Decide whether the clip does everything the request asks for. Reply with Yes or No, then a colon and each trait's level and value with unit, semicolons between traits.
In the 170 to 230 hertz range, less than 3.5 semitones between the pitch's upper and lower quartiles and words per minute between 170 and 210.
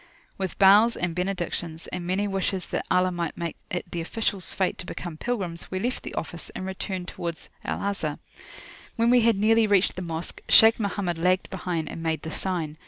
Yes: medium, 185 Hz; average, 2.9 semitones; average, 195 wpm